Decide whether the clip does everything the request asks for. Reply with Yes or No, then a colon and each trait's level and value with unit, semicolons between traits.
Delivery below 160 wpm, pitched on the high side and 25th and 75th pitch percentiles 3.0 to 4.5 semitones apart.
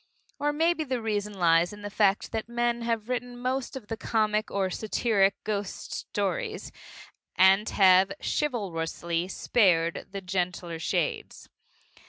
Yes: slow, 135 wpm; high, 210 Hz; average, 4.2 semitones